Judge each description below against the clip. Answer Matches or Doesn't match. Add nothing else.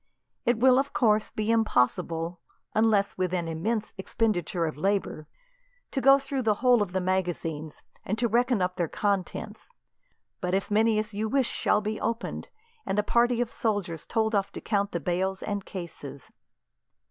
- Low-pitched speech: Doesn't match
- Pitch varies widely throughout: Doesn't match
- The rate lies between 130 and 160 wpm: Doesn't match